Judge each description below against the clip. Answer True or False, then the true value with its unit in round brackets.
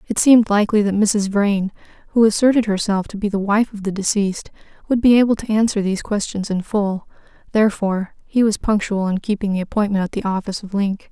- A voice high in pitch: True (205 Hz)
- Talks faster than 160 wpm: True (205 wpm)